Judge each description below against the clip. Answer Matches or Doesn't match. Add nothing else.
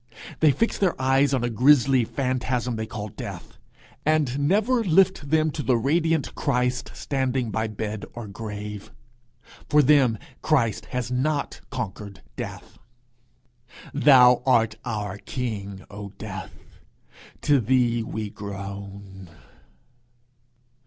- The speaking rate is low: Matches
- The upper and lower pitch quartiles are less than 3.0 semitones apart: Doesn't match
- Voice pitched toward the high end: Doesn't match